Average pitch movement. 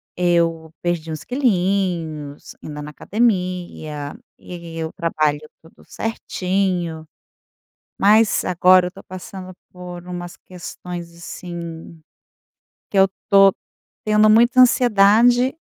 Yes: average, 3.1 semitones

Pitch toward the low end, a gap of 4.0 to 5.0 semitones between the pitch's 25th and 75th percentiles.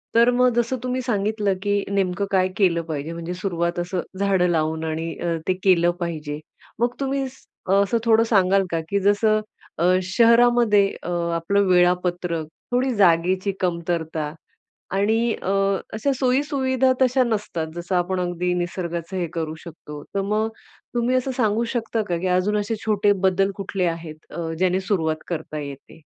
No: high, 190 Hz; average, 4.5 semitones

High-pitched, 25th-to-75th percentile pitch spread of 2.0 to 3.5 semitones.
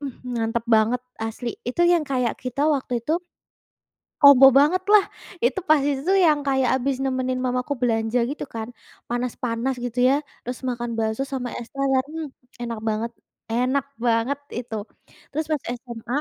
Yes: very high, 255 Hz; average, 2.9 semitones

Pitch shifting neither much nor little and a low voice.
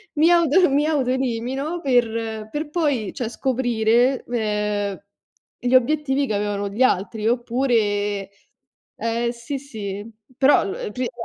No: average, 4.1 semitones; high, 240 Hz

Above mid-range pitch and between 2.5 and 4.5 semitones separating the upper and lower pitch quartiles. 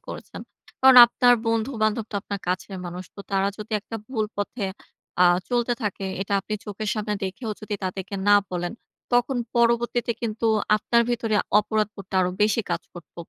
Yes: high, 215 Hz; average, 3.0 semitones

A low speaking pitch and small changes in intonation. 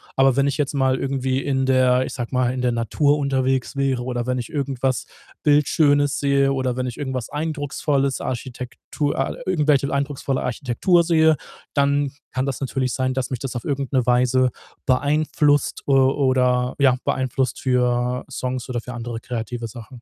Yes: low, 130 Hz; narrow, 1.9 semitones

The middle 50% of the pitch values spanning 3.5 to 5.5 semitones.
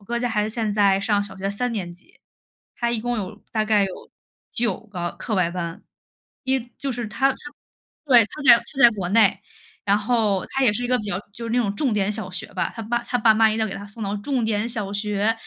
No: average, 2.9 semitones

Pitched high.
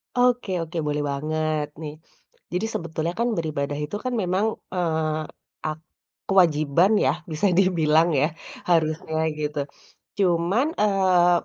No: medium, 165 Hz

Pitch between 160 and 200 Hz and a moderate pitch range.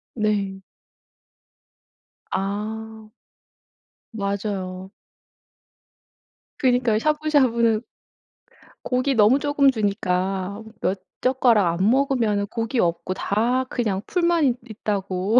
No: high, 220 Hz; average, 4.3 semitones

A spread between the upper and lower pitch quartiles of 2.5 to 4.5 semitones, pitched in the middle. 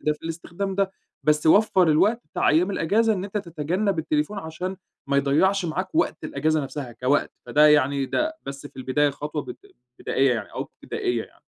No: average, 5.1 semitones; medium, 160 Hz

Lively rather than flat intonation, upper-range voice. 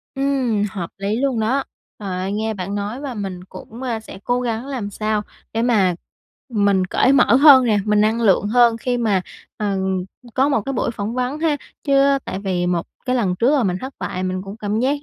No: average, 4.2 semitones; high, 220 Hz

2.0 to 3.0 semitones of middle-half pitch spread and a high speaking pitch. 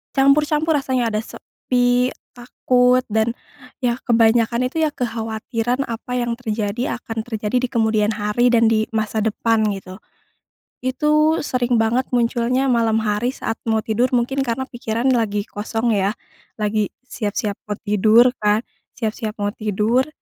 Yes: narrow, 2.4 semitones; high, 230 Hz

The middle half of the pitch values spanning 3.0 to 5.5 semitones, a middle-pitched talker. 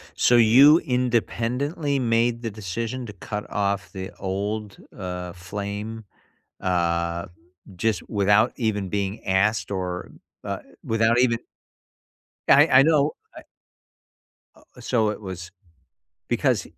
No: average, 3.6 semitones; low, 105 Hz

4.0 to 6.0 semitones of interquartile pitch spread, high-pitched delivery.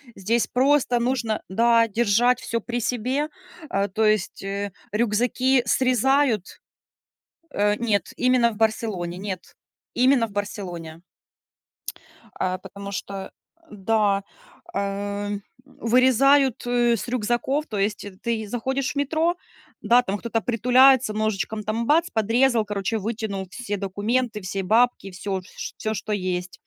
No: average, 3.6 semitones; high, 220 Hz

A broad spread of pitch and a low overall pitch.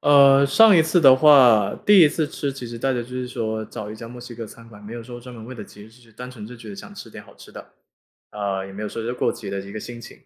No: average, 3.6 semitones; low, 120 Hz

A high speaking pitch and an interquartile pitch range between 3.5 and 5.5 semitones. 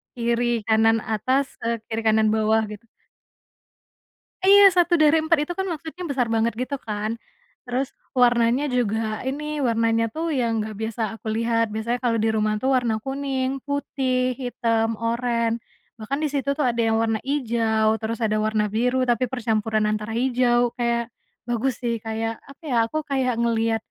No: high, 235 Hz; average, 2.9 semitones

